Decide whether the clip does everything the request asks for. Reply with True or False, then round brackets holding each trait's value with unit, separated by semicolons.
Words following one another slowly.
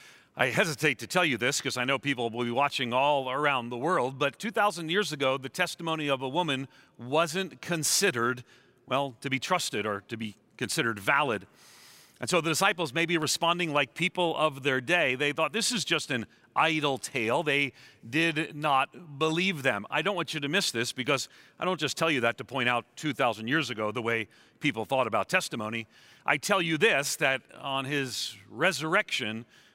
False (195 wpm)